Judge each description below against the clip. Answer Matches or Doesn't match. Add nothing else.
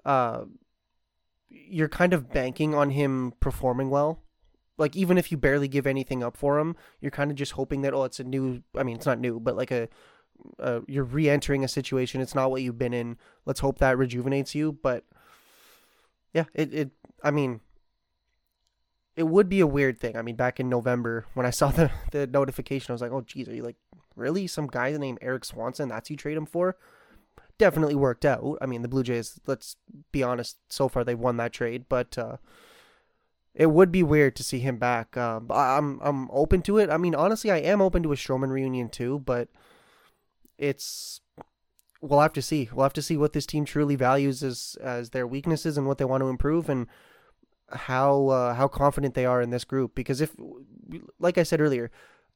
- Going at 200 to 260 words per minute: Matches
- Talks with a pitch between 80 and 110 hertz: Doesn't match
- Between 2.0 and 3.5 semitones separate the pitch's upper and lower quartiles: Matches